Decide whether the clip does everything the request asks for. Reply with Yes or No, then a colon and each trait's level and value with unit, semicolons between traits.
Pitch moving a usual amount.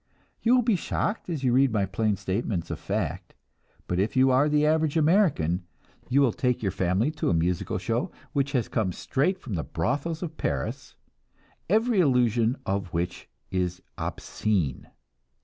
No: wide, 8.3 semitones